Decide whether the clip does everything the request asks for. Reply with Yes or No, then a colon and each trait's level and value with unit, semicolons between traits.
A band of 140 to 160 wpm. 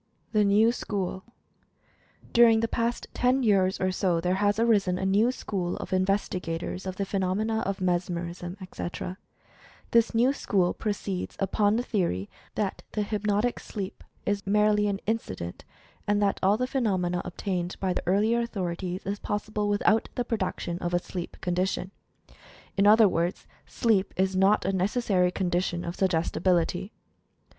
Yes: average, 155 wpm